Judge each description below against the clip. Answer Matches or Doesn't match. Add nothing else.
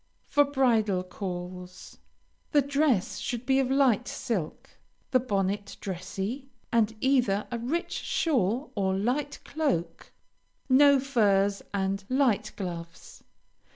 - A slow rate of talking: Matches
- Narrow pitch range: Doesn't match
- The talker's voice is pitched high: Matches